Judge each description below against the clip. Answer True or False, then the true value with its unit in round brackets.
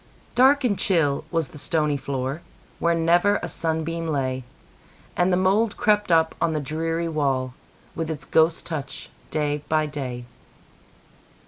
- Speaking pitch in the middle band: True (160 Hz)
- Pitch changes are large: False (3.0 semitones)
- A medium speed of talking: False (130 wpm)